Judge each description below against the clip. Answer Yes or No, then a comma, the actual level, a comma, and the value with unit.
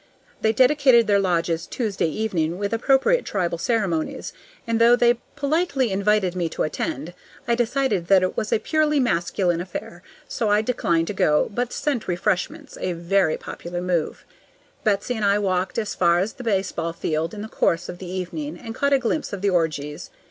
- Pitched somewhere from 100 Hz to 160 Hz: No, high, 200 Hz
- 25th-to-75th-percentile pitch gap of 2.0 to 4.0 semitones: No, wide, 5.4 semitones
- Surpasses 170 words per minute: Yes, average, 185 wpm